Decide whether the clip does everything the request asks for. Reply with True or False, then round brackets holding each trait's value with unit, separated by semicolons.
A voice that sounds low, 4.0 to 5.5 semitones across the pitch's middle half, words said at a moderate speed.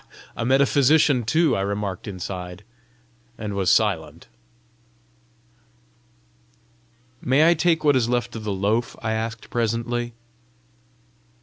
False (115 Hz; 4.3 semitones; 110 wpm)